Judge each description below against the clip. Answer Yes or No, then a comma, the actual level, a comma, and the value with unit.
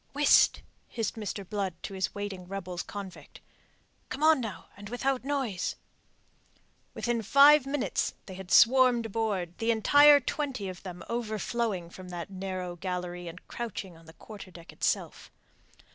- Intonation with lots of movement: No, average, 4.8 semitones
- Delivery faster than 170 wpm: No, average, 145 wpm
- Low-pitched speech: No, high, 205 Hz